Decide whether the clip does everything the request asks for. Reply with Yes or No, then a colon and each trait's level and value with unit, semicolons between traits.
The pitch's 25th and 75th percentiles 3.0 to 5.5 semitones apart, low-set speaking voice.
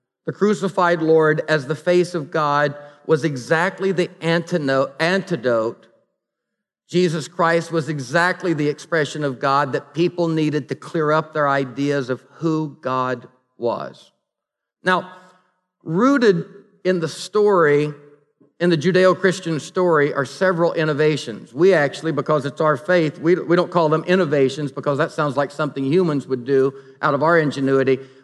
No: average, 3.6 semitones; medium, 155 Hz